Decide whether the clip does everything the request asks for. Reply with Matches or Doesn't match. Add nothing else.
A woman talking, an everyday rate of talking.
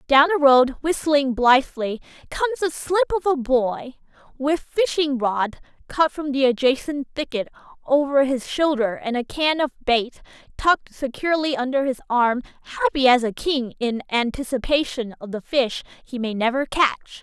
Matches